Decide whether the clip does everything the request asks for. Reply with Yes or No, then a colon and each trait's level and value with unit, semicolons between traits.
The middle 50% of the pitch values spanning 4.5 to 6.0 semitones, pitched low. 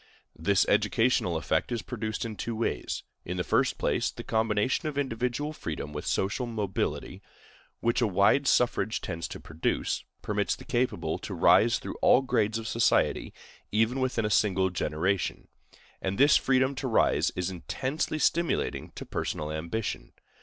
Yes: average, 5.2 semitones; low, 110 Hz